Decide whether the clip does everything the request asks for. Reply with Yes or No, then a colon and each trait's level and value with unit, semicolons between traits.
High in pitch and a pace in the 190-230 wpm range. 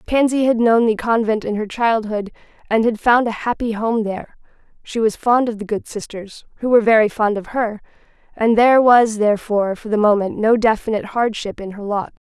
Yes: high, 220 Hz; average, 200 wpm